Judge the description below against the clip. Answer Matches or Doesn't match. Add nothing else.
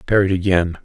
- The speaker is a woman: Doesn't match